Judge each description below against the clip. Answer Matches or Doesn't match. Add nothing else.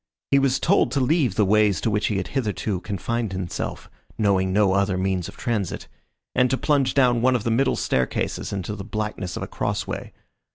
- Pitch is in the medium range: Doesn't match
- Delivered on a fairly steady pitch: Doesn't match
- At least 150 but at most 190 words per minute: Doesn't match